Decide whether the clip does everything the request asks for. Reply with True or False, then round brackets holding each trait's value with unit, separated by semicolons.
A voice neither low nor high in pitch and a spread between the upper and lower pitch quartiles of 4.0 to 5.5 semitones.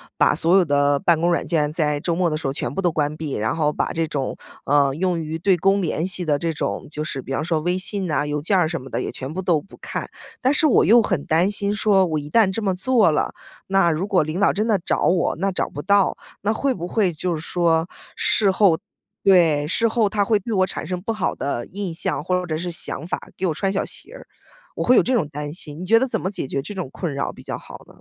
True (175 Hz; 4.3 semitones)